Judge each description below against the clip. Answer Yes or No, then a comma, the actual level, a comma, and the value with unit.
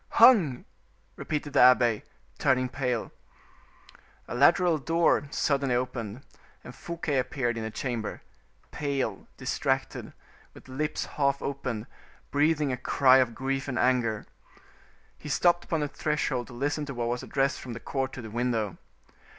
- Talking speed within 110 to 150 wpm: Yes, average, 145 wpm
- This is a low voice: Yes, low, 130 Hz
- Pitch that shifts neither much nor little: Yes, average, 3.1 semitones